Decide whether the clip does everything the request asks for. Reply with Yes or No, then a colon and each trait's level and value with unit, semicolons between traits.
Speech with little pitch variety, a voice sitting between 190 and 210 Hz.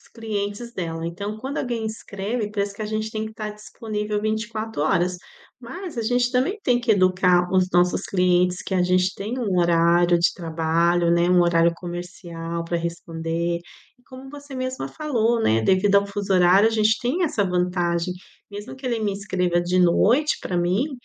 No: average, 4.2 semitones; high, 195 Hz